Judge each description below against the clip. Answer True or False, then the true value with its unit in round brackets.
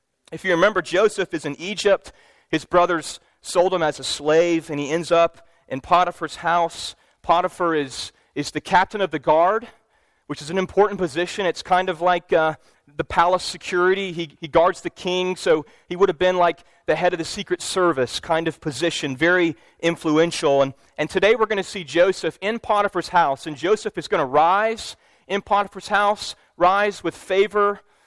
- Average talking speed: True (185 wpm)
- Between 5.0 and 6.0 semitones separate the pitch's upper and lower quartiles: False (2.7 semitones)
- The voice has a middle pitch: True (175 Hz)